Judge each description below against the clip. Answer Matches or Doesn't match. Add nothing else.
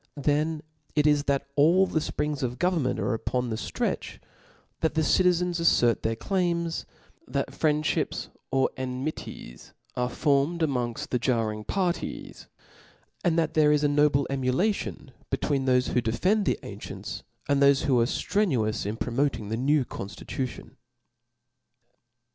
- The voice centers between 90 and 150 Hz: Matches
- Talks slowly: Doesn't match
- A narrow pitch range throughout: Doesn't match